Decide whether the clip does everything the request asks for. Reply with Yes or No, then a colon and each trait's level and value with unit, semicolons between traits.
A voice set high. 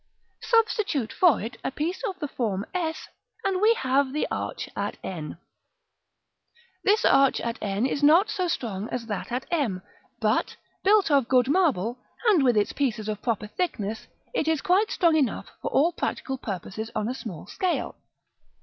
Yes: very high, 270 Hz